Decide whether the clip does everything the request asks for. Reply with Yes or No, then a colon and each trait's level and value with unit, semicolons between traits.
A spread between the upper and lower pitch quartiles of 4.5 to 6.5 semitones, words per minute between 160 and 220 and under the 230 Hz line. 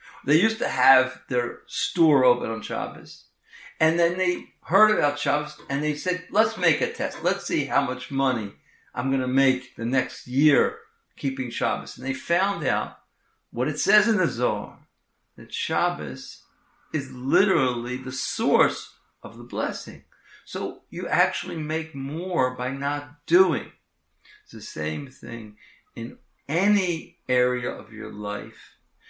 No: average, 5.1 semitones; average, 150 wpm; medium, 140 Hz